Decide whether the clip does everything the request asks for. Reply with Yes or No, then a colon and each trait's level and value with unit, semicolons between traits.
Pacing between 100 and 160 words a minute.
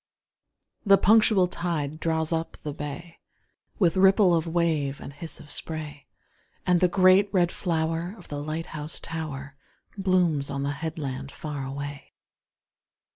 Yes: average, 140 wpm